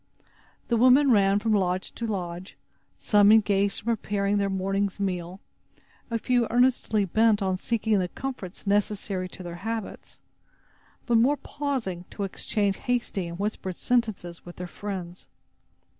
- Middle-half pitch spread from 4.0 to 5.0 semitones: No, average, 3.4 semitones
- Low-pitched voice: No, high, 205 Hz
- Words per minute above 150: No, average, 145 wpm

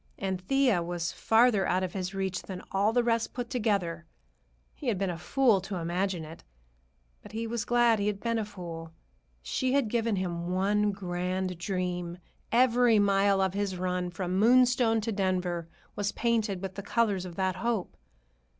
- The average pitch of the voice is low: No, high, 195 Hz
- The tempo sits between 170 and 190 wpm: Yes, average, 180 wpm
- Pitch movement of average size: Yes, average, 3.9 semitones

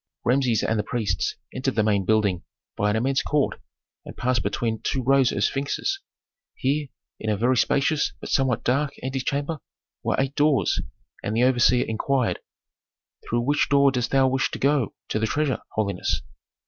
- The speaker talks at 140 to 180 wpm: Yes, average, 170 wpm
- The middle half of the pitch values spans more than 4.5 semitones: No, average, 3.7 semitones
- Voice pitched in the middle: No, low, 130 Hz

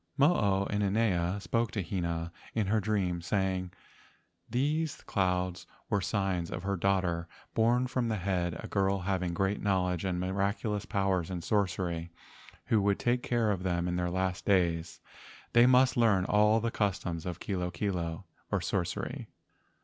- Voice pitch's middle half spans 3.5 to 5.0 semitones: No, average, 2.9 semitones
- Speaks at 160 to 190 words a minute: Yes, average, 165 wpm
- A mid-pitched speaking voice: No, very low, 95 Hz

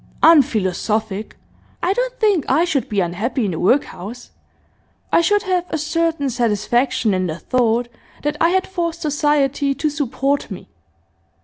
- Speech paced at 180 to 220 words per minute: No, average, 145 wpm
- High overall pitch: Yes, very high, 275 Hz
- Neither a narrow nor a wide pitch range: No, wide, 7.0 semitones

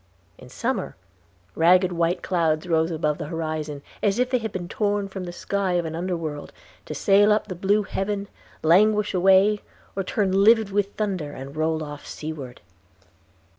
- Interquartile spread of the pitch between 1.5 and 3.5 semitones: No, average, 4.0 semitones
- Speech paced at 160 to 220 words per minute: Yes, average, 170 wpm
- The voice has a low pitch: No, medium, 180 Hz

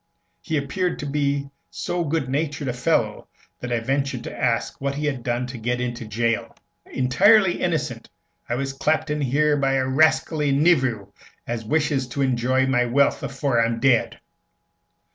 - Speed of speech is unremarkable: Yes, average, 165 wpm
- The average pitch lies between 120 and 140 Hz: Yes, low, 135 Hz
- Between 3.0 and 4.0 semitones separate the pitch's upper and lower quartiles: Yes, average, 3.3 semitones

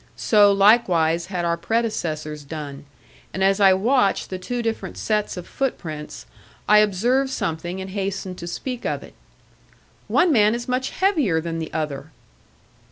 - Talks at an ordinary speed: Yes, average, 155 wpm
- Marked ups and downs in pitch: Yes, wide, 5.7 semitones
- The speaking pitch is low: No, high, 190 Hz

